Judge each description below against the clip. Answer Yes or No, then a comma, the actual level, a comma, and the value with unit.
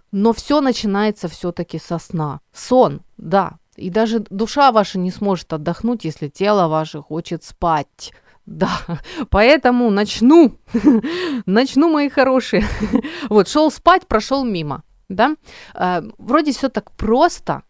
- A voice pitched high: Yes, high, 215 Hz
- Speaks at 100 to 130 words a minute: Yes, average, 120 wpm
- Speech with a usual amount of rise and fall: No, wide, 6.6 semitones